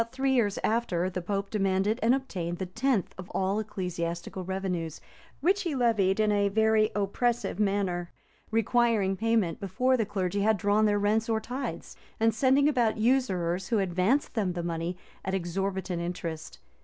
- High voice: Yes, high, 205 Hz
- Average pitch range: Yes, average, 3.7 semitones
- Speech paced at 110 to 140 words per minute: No, average, 165 wpm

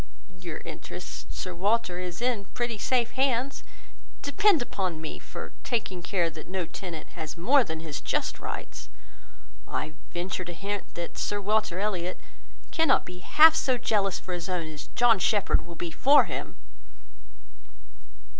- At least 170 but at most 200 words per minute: No, average, 155 wpm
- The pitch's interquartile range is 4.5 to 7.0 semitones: Yes, wide, 5.5 semitones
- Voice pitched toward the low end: No, high, 190 Hz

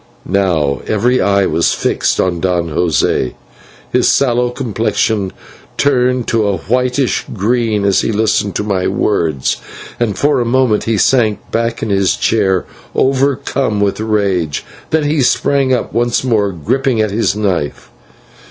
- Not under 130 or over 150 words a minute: Yes, average, 145 wpm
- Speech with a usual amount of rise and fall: Yes, average, 4.4 semitones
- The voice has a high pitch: No, low, 110 Hz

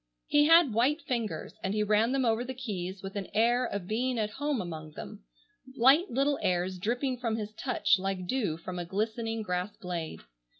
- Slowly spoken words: No, average, 195 wpm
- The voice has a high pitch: Yes, high, 220 Hz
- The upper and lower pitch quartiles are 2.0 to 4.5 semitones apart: No, average, 5.2 semitones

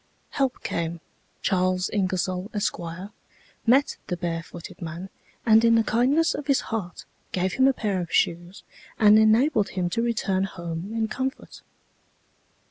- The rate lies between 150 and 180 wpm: No, average, 140 wpm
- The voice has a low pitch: No, high, 200 Hz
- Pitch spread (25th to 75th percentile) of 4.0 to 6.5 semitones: Yes, average, 4.4 semitones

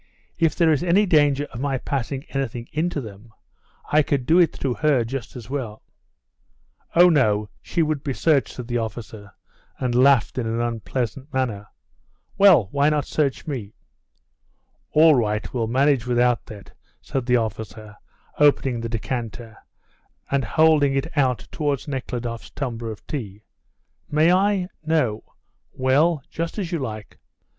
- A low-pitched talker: Yes, low, 130 Hz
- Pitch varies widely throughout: No, average, 4.6 semitones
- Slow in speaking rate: No, average, 150 wpm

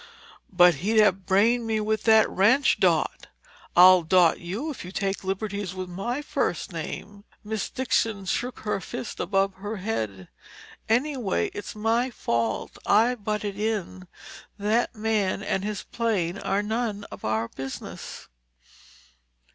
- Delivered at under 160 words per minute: Yes, average, 140 wpm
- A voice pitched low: No, high, 205 Hz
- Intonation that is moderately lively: Yes, average, 3.1 semitones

